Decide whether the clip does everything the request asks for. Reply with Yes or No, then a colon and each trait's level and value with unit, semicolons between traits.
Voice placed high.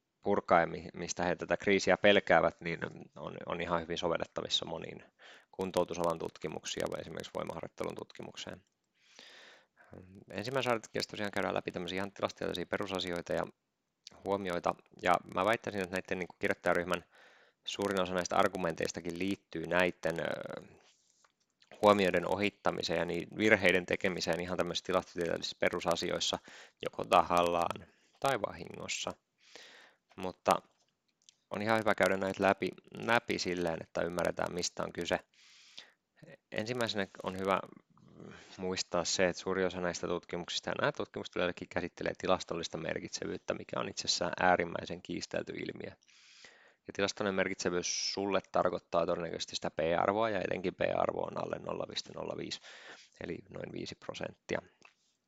No: very low, 95 Hz